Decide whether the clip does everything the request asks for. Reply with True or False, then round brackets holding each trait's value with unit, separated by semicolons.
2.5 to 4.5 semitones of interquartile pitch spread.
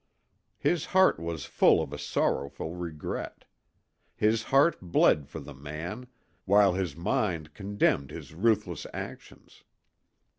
False (5.6 semitones)